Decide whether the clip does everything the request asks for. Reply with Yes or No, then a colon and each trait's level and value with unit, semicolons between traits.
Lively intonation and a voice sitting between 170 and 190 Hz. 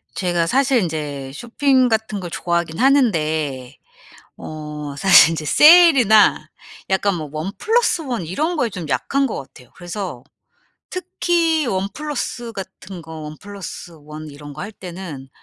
Yes: wide, 8.2 semitones; medium, 185 Hz